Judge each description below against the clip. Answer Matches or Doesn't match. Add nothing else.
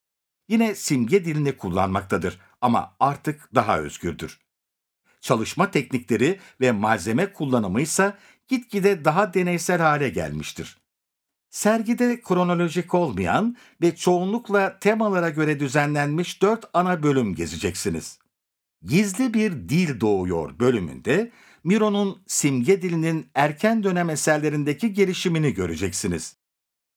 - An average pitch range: Doesn't match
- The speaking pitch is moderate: Matches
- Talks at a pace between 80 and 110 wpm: Matches